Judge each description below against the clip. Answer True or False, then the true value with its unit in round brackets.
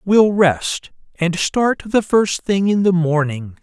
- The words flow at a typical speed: True (165 wpm)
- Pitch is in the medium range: True (180 Hz)